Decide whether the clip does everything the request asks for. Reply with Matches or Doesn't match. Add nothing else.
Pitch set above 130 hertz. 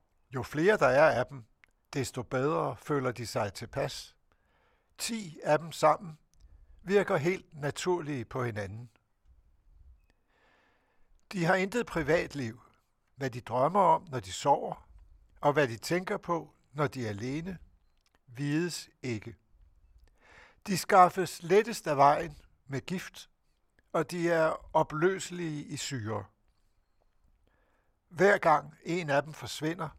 Matches